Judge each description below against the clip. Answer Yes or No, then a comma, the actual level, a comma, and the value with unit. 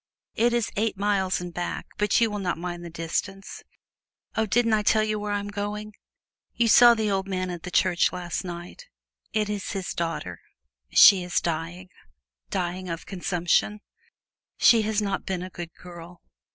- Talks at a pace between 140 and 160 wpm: No, average, 175 wpm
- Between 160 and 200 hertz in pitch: Yes, high, 190 Hz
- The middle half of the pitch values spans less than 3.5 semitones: Yes, average, 3.1 semitones